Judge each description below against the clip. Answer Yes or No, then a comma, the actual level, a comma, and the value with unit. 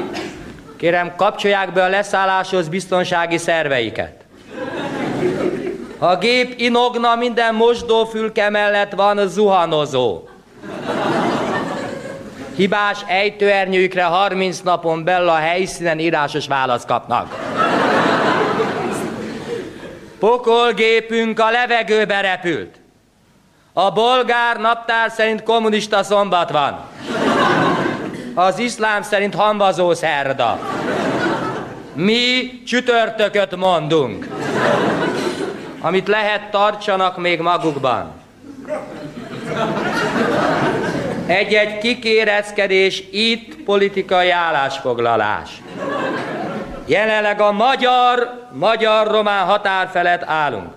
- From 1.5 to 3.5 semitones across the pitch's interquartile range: No, average, 4.2 semitones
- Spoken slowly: Yes, slow, 70 wpm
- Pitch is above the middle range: Yes, high, 200 Hz